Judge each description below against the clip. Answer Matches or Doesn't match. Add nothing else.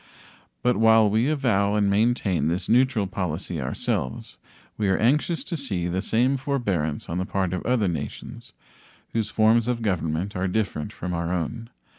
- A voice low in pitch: Matches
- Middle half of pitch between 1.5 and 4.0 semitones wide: Doesn't match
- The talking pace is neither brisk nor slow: Matches